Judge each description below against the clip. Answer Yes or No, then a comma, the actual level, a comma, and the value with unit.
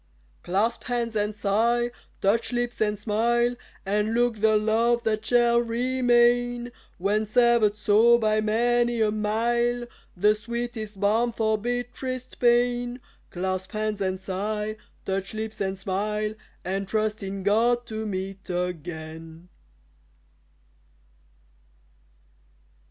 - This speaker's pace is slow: Yes, slow, 115 wpm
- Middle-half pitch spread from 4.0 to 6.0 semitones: No, average, 2.8 semitones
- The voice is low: No, high, 220 Hz